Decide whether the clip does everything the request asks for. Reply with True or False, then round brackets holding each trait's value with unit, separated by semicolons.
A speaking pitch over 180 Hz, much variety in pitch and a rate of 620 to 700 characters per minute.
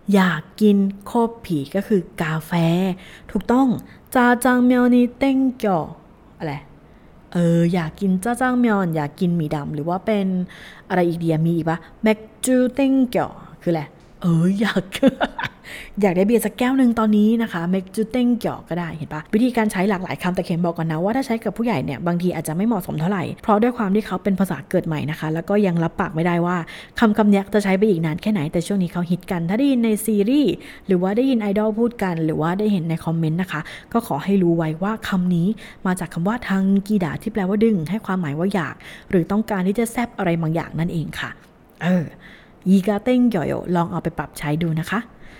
False (190 Hz; 4.4 semitones; 635 characters per minute)